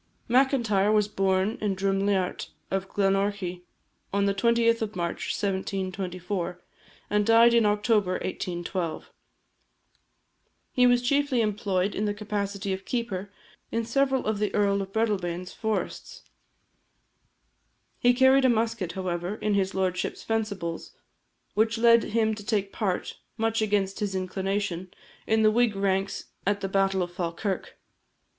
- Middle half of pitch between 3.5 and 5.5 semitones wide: No, average, 2.8 semitones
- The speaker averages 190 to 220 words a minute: No, slow, 135 wpm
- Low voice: No, high, 200 Hz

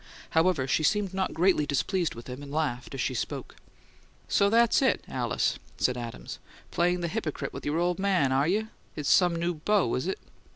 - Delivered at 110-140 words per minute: No, average, 195 wpm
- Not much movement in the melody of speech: No, wide, 5.4 semitones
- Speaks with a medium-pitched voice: Yes, medium, 170 Hz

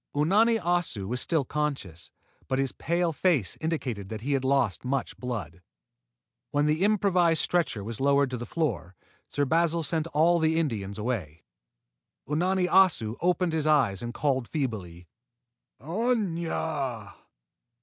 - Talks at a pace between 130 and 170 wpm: Yes, average, 140 wpm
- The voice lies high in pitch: No, medium, 145 Hz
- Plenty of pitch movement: Yes, wide, 6.4 semitones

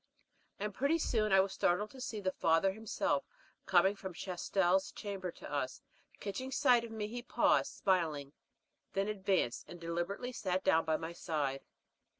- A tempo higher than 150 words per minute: Yes, average, 160 wpm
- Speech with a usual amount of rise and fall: Yes, average, 3.7 semitones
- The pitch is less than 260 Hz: Yes, high, 190 Hz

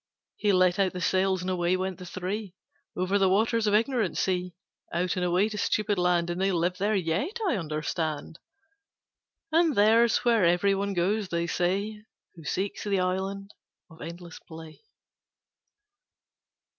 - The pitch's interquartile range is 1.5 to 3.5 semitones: Yes, average, 2.7 semitones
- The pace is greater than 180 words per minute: No, average, 155 wpm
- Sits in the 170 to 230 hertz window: Yes, medium, 185 Hz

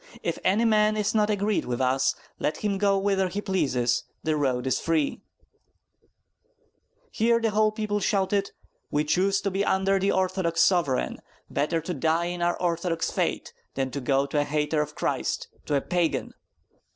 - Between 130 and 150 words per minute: No, average, 175 wpm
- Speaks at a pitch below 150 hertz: No, medium, 180 Hz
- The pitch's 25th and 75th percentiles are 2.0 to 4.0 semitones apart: No, average, 5.2 semitones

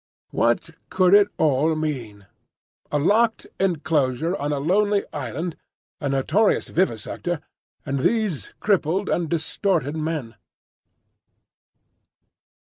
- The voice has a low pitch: No, medium, 160 Hz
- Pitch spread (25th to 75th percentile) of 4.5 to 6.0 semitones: Yes, average, 5.1 semitones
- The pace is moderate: No, slow, 100 wpm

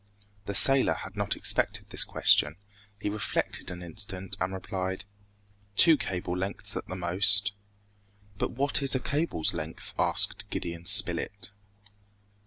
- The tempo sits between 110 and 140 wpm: Yes, slow, 135 wpm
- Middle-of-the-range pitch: No, very low, 95 Hz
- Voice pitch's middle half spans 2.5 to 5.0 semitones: Yes, average, 2.9 semitones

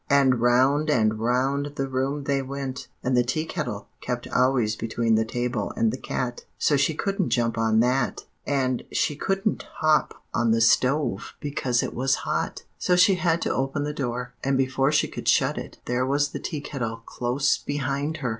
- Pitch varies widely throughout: No, average, 3.0 semitones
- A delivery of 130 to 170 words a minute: No, average, 190 wpm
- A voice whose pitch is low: Yes, low, 130 Hz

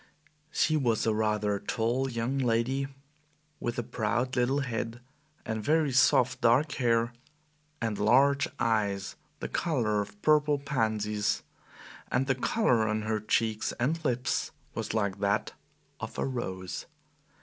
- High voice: No, low, 115 Hz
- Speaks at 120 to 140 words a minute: Yes, slow, 135 wpm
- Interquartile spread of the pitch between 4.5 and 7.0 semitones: No, average, 3.7 semitones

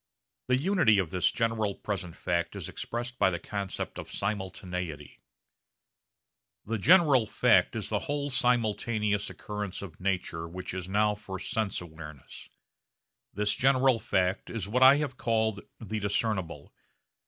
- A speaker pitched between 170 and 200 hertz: No, low, 105 Hz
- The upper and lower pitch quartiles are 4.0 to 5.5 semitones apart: Yes, average, 4.3 semitones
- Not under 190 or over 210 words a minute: No, average, 140 wpm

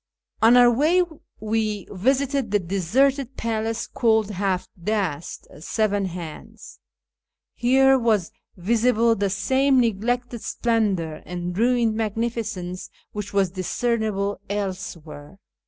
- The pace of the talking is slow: Yes, slow, 110 wpm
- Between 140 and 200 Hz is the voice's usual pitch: No, high, 220 Hz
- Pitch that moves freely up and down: No, average, 3.9 semitones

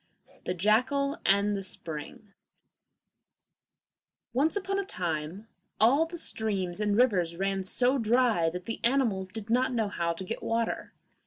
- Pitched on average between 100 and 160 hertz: No, high, 215 Hz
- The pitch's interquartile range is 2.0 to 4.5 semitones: No, average, 5.1 semitones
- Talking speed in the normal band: Yes, average, 150 wpm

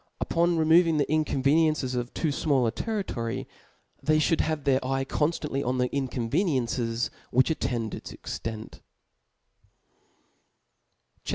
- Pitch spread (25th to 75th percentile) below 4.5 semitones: Yes, average, 3.9 semitones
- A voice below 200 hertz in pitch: Yes, medium, 140 Hz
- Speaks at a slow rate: Yes, slow, 125 wpm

